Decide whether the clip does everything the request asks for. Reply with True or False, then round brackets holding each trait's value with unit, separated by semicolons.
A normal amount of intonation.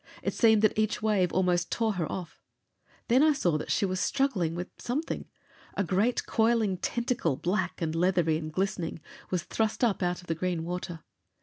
True (4.1 semitones)